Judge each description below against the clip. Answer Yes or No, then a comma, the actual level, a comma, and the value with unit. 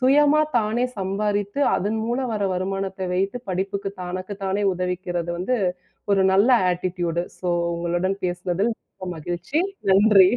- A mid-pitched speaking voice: No, high, 195 Hz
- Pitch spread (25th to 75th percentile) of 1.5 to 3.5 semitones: Yes, narrow, 2.6 semitones